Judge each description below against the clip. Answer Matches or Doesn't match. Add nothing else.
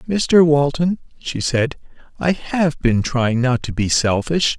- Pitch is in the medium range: Matches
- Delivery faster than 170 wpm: Doesn't match